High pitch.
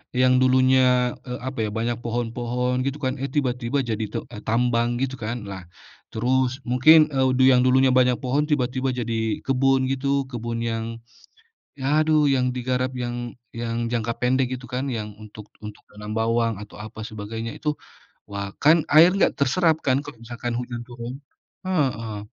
No: low, 125 Hz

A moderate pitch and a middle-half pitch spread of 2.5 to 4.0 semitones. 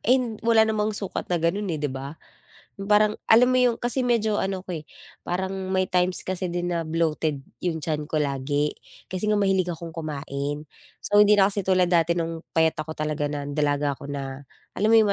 No: medium, 175 Hz; average, 5.0 semitones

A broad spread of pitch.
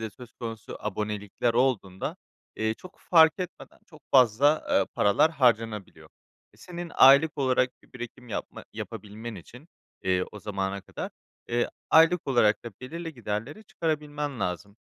Yes: wide, 6.1 semitones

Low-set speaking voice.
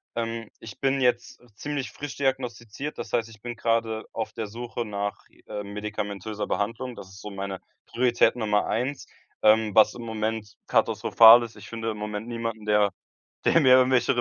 Yes: low, 115 Hz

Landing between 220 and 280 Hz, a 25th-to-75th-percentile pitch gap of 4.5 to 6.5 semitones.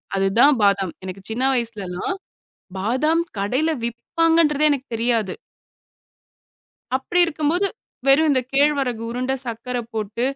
Yes: very high, 250 Hz; average, 5.2 semitones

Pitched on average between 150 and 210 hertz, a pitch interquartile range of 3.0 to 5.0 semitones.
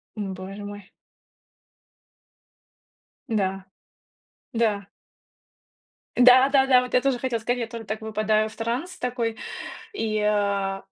No: high, 220 Hz; average, 3.4 semitones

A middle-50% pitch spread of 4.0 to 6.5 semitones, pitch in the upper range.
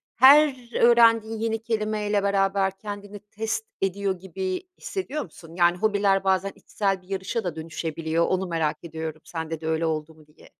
Yes: average, 4.6 semitones; high, 195 Hz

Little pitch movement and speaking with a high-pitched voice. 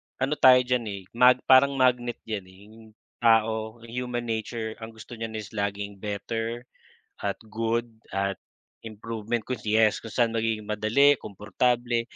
No: narrow, 2.0 semitones; low, 115 Hz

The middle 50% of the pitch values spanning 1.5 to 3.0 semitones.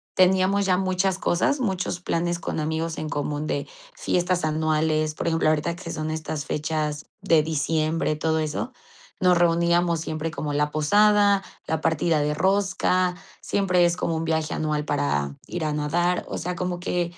Yes: average, 2.7 semitones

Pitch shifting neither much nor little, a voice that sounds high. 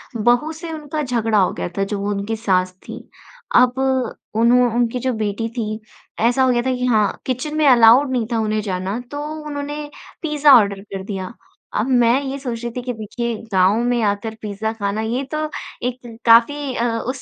Yes: average, 3.3 semitones; high, 235 Hz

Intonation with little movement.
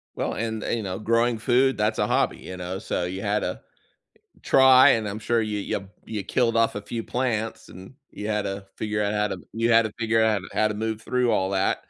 Yes: narrow, 2.2 semitones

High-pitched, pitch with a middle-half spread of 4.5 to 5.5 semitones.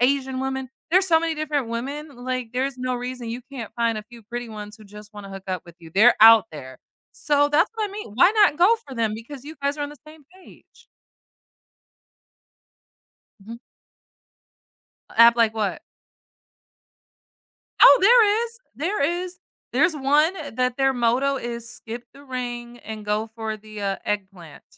Yes: very high, 250 Hz; average, 4.9 semitones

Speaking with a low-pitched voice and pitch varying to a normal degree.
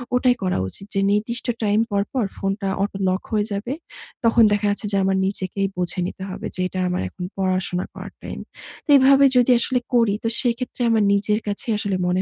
No: high, 205 Hz; average, 3.4 semitones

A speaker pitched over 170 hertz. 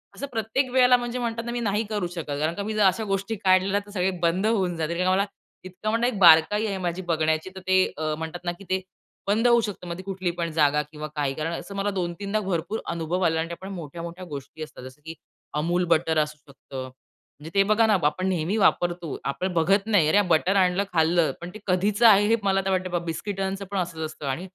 Yes: medium, 185 Hz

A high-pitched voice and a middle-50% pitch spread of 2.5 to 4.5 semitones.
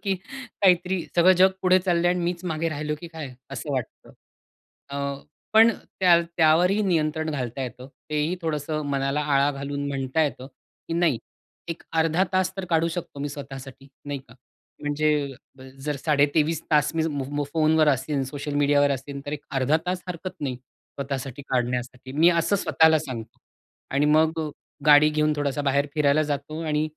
No: medium, 150 Hz; average, 2.8 semitones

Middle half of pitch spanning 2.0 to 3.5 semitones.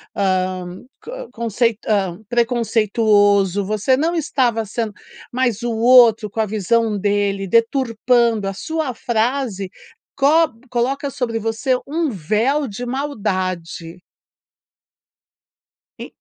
No: average, 4.0 semitones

